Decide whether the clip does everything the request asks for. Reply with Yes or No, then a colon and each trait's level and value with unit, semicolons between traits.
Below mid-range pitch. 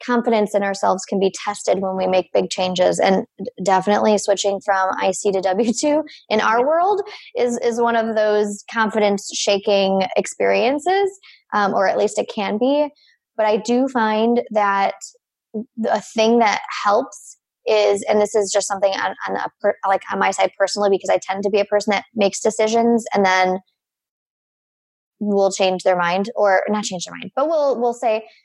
No: high, 210 Hz